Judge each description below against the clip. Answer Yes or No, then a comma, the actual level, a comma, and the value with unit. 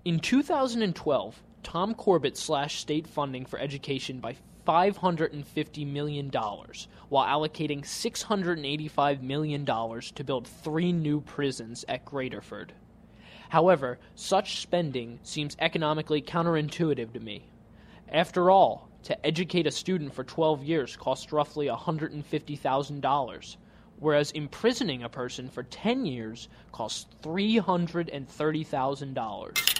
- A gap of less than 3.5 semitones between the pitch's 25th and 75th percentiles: No, average, 4.2 semitones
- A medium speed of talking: No, slow, 105 wpm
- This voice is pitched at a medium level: Yes, medium, 150 Hz